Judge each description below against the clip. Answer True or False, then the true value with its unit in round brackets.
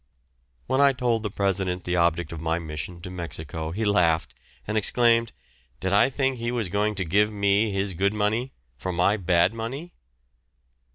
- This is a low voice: True (100 Hz)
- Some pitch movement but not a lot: True (4.5 semitones)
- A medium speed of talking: True (175 wpm)